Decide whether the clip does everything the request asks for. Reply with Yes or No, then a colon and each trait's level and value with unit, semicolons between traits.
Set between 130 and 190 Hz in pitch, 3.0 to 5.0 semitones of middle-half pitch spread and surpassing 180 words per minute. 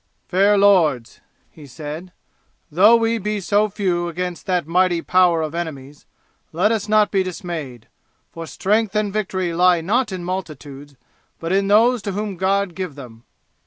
No: medium, 185 Hz; average, 3.6 semitones; average, 160 wpm